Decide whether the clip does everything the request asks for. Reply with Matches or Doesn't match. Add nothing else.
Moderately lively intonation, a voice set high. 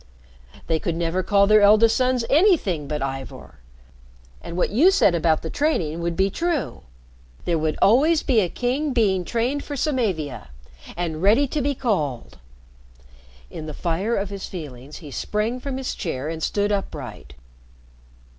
Doesn't match